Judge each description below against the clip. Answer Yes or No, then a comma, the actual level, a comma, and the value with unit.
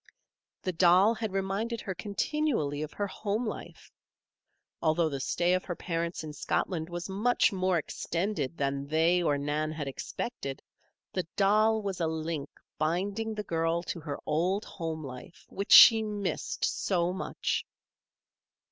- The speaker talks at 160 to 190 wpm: No, average, 145 wpm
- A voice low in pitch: No, medium, 175 Hz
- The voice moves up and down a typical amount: Yes, average, 4.3 semitones